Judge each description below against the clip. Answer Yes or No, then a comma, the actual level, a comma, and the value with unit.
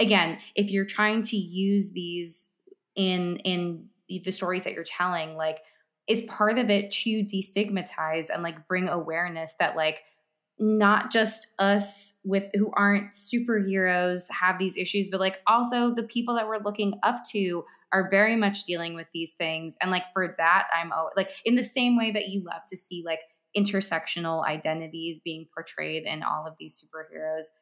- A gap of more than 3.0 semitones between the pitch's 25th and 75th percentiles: Yes, average, 3.8 semitones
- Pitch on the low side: No, high, 190 Hz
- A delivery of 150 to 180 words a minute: Yes, average, 175 wpm